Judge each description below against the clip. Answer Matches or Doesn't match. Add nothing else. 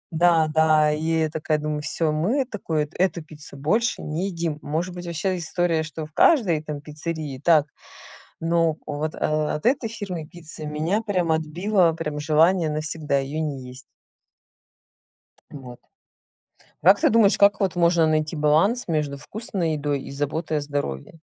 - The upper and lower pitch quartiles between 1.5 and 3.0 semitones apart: Matches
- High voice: Doesn't match